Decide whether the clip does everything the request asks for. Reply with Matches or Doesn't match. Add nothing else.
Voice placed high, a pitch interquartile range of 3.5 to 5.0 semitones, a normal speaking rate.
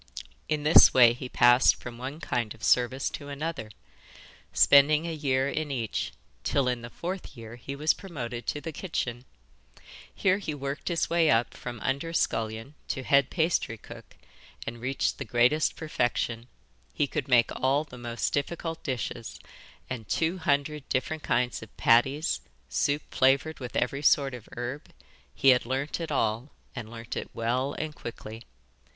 Doesn't match